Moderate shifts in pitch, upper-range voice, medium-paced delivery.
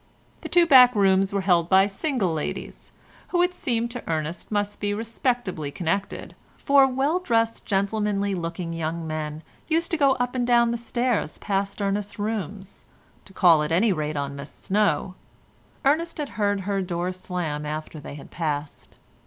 No: wide, 6.1 semitones; high, 200 Hz; average, 160 wpm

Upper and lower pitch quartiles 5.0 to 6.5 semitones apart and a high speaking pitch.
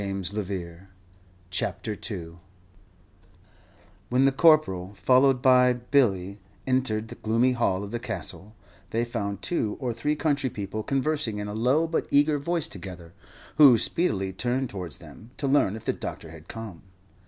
No: wide, 5.4 semitones; low, 115 Hz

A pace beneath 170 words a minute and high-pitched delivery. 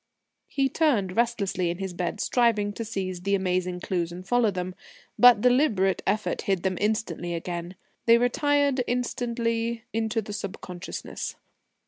Yes: average, 140 wpm; high, 205 Hz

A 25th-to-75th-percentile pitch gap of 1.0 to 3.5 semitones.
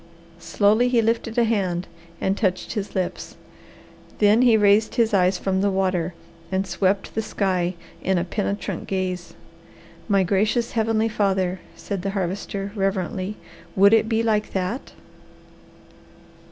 Yes: narrow, 2.6 semitones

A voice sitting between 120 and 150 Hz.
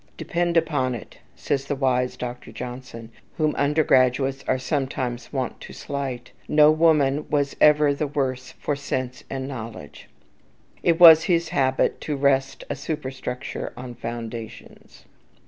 Yes: low, 135 Hz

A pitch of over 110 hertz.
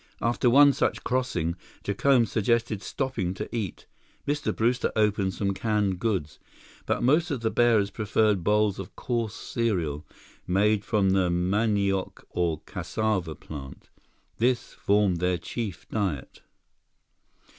No: low, 105 Hz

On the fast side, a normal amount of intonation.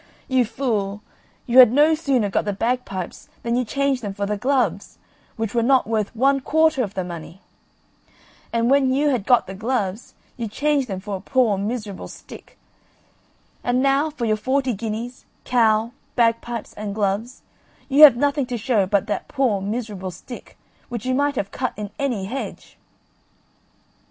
No: average, 170 wpm; average, 4.2 semitones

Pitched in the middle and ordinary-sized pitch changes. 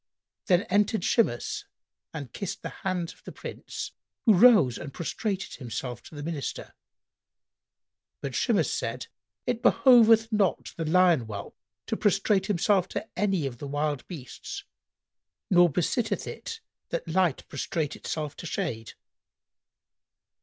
No: medium, 175 Hz; wide, 6.2 semitones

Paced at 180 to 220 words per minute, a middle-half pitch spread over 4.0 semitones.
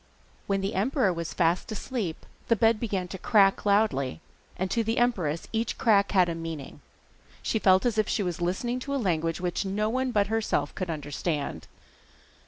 Yes: average, 185 wpm; average, 4.6 semitones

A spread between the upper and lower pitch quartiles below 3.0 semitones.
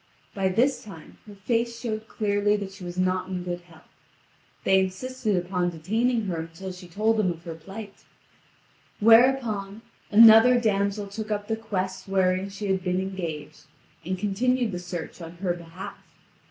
No: average, 3.3 semitones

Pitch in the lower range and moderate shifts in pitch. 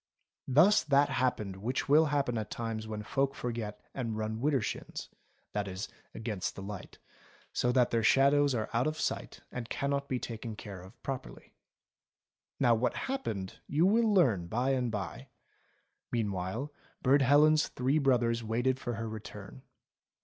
Yes: low, 120 Hz; average, 4.2 semitones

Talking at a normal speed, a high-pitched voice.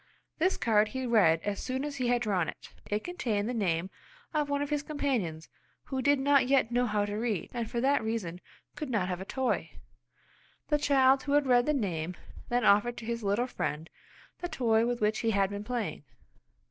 No: fast, 210 wpm; high, 235 Hz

